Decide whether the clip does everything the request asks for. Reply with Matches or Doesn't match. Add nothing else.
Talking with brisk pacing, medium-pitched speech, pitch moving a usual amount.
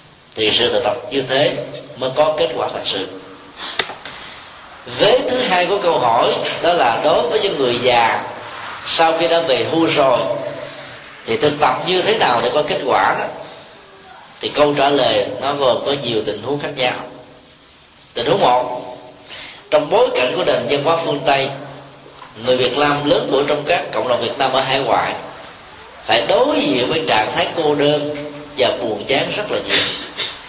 Doesn't match